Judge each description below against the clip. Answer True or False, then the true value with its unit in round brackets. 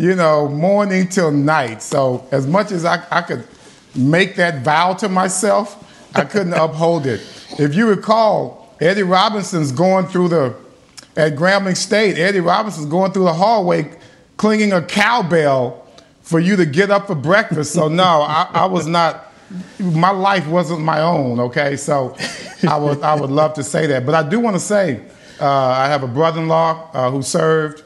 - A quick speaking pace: False (180 wpm)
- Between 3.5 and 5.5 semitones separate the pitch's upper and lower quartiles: True (4.0 semitones)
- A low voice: False (170 Hz)